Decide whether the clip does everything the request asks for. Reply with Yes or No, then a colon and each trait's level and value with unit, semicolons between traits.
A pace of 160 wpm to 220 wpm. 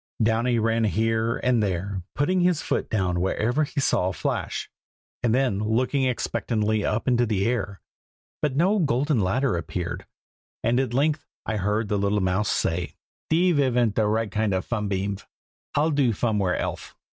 Yes: average, 165 wpm